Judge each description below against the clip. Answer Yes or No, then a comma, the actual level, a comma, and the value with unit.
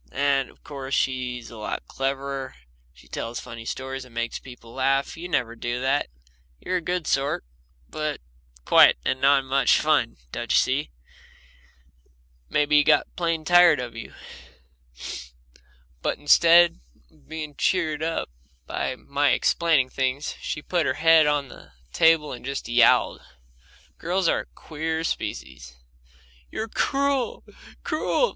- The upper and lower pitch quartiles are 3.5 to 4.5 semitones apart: Yes, average, 4.0 semitones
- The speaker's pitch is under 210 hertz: Yes, medium, 140 Hz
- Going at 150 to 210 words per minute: No, average, 140 wpm